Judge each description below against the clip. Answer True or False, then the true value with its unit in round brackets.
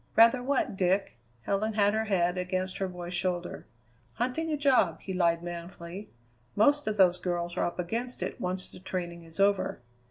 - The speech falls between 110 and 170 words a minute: False (180 wpm)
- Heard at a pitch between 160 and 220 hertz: True (185 Hz)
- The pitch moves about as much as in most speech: True (3.7 semitones)